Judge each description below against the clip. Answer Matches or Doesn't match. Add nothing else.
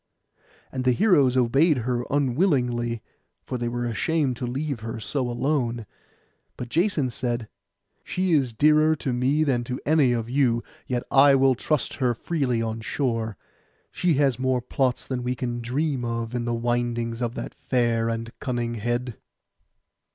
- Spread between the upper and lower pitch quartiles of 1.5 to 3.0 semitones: Matches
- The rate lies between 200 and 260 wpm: Doesn't match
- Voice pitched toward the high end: Doesn't match